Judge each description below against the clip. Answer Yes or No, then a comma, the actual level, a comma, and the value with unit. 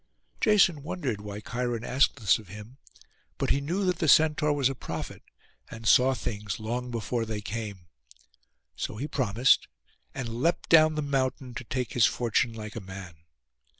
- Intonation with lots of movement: No, average, 4.6 semitones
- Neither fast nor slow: Yes, average, 170 wpm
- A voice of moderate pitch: No, low, 125 Hz